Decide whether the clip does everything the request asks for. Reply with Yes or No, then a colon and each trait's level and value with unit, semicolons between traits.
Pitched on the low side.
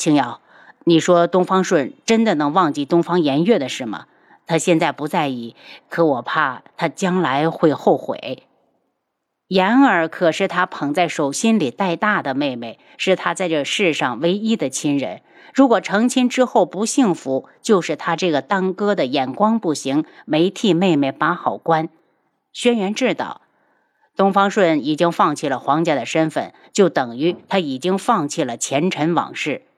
No: medium, 175 Hz